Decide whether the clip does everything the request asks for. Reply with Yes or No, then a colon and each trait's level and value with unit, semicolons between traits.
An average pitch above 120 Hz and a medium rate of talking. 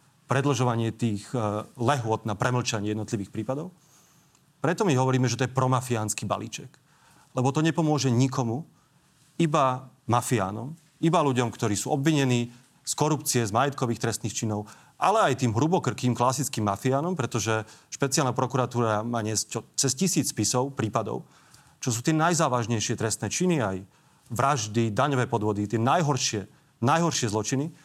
Yes: low, 130 Hz; average, 130 wpm